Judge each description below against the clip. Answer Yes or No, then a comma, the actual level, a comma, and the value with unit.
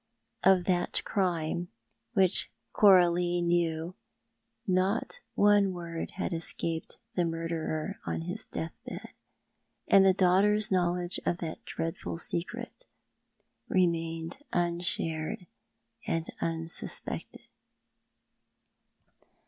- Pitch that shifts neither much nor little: No, narrow, 2.1 semitones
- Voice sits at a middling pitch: Yes, medium, 175 Hz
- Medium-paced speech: No, slow, 90 wpm